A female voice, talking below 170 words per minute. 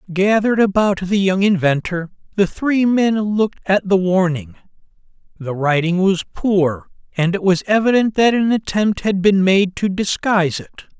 No: male; average, 160 wpm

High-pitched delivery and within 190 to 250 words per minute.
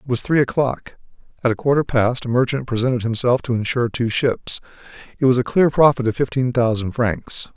No: low, 125 Hz; average, 200 wpm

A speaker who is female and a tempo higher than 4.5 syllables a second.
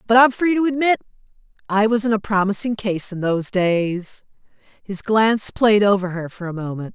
Yes: female; 5.0 syllables/s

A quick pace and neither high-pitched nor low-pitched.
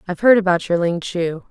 Yes: fast, 240 wpm; medium, 180 Hz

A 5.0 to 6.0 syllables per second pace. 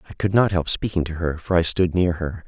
Yes: 5.9 syllables/s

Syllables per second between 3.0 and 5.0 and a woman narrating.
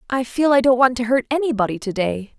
No: 6.0 syllables/s; female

